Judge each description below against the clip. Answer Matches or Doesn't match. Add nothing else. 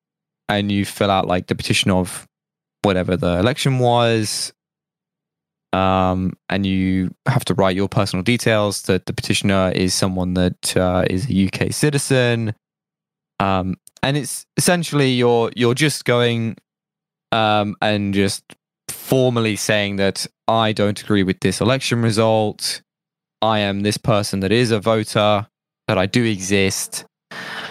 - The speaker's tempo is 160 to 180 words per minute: Doesn't match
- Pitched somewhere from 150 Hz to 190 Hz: Doesn't match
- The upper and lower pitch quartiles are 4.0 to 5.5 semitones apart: Matches